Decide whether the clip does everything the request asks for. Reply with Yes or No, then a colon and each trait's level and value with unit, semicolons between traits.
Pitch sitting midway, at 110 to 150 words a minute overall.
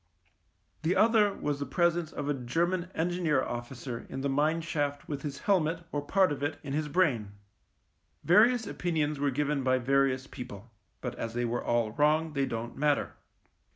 No: medium, 145 Hz; average, 175 wpm